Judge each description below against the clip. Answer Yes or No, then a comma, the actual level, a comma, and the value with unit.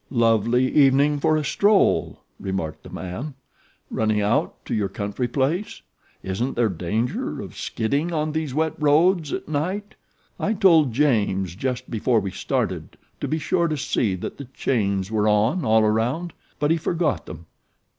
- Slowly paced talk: No, average, 160 wpm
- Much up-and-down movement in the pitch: Yes, wide, 6.4 semitones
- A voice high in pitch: No, low, 130 Hz